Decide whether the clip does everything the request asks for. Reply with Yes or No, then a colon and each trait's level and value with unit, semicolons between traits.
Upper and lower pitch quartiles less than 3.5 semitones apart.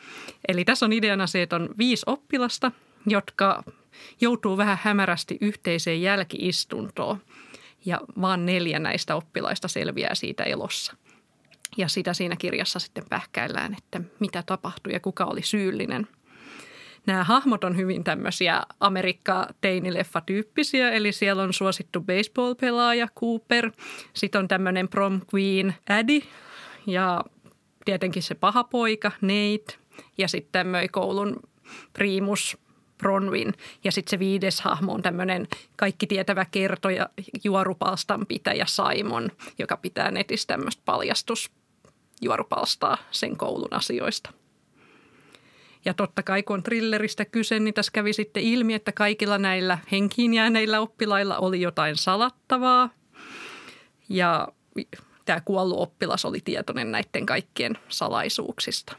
Yes: narrow, 2.6 semitones